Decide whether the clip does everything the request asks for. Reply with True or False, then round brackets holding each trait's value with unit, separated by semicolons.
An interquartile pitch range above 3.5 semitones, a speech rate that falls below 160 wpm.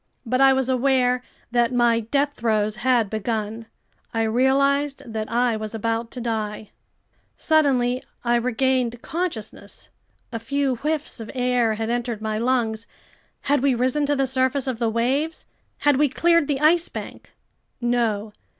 False (3.2 semitones; 150 wpm)